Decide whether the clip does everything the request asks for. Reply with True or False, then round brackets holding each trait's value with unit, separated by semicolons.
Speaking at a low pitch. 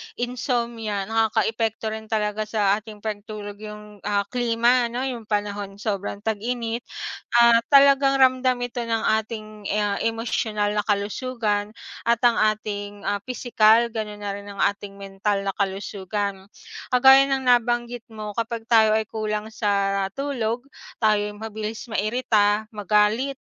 False (220 Hz)